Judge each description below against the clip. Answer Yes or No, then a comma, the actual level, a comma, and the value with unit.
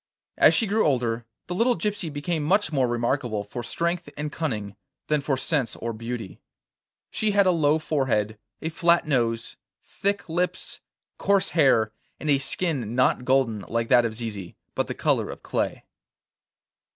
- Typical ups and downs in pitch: No, wide, 6.5 semitones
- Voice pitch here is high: No, medium, 140 Hz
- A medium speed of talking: Yes, average, 165 wpm